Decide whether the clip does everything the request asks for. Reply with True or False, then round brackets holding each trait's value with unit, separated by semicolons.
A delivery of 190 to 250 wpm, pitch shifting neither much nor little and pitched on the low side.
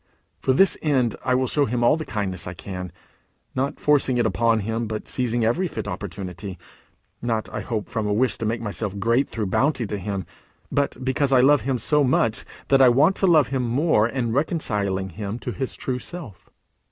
True (200 wpm; 4.4 semitones; 120 Hz)